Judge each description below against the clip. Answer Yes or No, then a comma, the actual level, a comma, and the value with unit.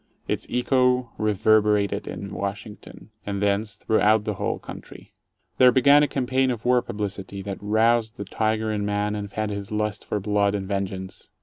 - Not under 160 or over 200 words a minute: Yes, average, 170 wpm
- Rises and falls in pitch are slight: Yes, narrow, 2.1 semitones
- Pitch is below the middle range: Yes, low, 105 Hz